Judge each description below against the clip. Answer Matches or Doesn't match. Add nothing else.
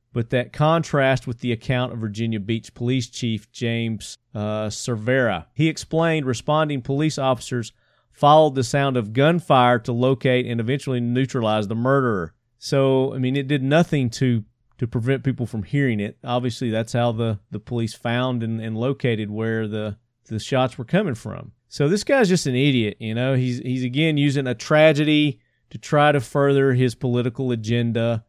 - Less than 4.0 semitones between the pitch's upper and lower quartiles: Matches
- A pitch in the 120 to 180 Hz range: Matches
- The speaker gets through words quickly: Doesn't match